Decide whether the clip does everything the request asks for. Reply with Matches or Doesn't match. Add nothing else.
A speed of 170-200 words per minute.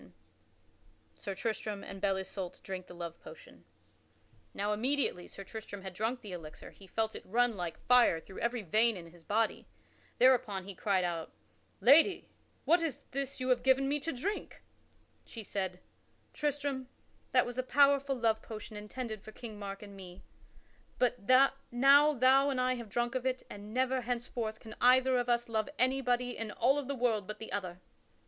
Matches